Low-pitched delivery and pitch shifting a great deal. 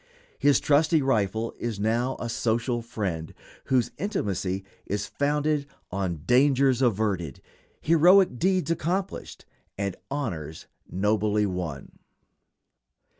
Yes: low, 115 Hz; wide, 6.5 semitones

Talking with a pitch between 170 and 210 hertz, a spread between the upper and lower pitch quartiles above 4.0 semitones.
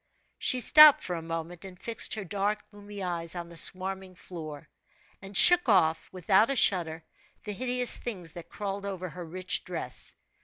No: medium, 185 Hz; average, 3.3 semitones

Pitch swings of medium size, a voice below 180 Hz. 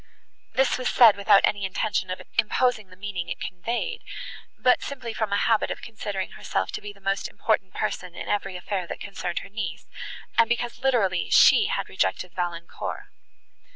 No: average, 4.0 semitones; high, 205 Hz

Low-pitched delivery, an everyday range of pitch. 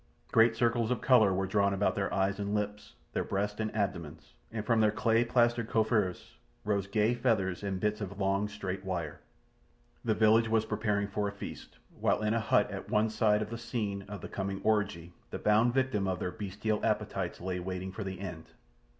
No: low, 105 Hz; narrow, 2.3 semitones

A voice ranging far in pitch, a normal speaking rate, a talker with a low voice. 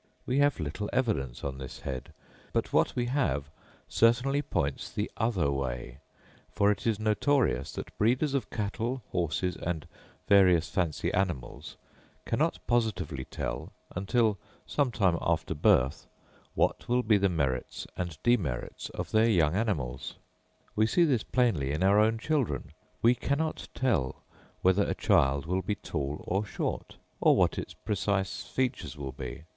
Yes: wide, 8.3 semitones; average, 150 wpm; low, 100 Hz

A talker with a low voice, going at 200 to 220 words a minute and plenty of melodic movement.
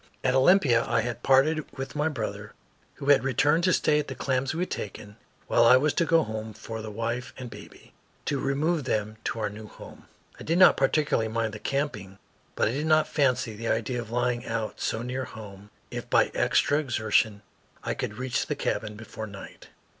No: low, 125 Hz; fast, 205 wpm; average, 4.6 semitones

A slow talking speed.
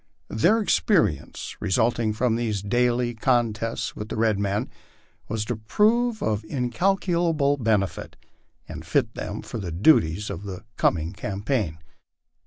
Yes: slow, 130 wpm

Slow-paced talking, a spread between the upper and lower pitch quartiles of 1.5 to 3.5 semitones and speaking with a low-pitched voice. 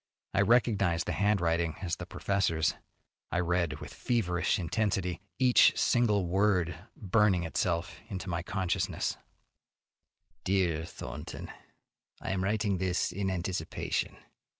Yes: slow, 115 wpm; average, 2.7 semitones; very low, 95 Hz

